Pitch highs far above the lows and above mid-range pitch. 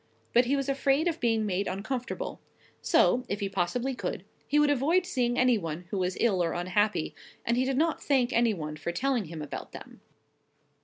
Yes: wide, 6.5 semitones; high, 240 Hz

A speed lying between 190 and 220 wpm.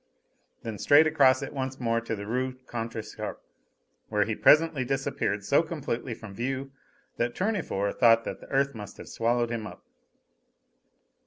No: average, 155 wpm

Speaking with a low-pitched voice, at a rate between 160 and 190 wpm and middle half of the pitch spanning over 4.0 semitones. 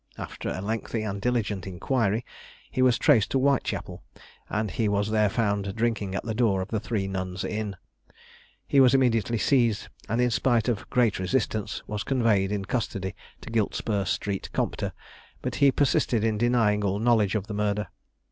No: low, 110 Hz; average, 175 wpm; average, 2.9 semitones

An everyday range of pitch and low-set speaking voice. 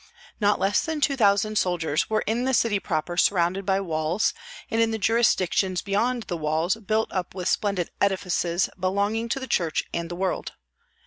No: average, 4.0 semitones; high, 195 Hz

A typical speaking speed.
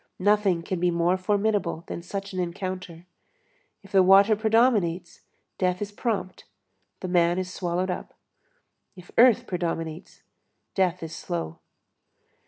No: slow, 130 wpm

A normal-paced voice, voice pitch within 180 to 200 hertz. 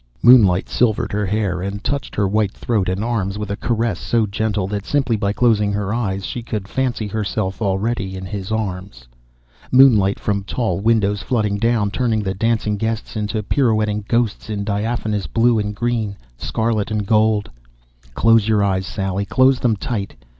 No: average, 170 wpm; low, 105 Hz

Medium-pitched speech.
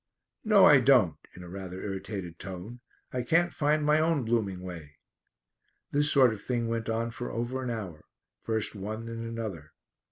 No: low, 115 Hz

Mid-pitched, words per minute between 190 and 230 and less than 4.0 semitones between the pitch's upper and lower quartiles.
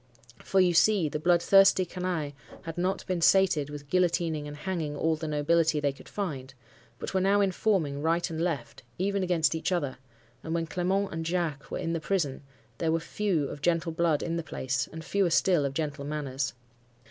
Yes: medium, 165 Hz; average, 195 wpm; average, 3.5 semitones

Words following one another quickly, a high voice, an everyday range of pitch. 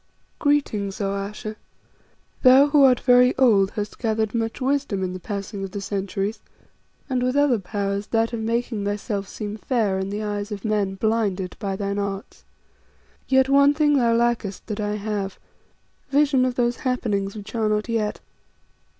No: average, 165 wpm; high, 215 Hz; average, 3.7 semitones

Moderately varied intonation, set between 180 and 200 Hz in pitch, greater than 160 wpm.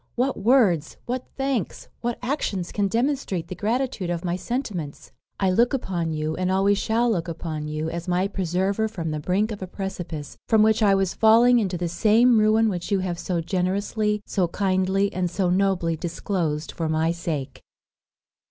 Yes: average, 4.1 semitones; high, 190 Hz; average, 180 wpm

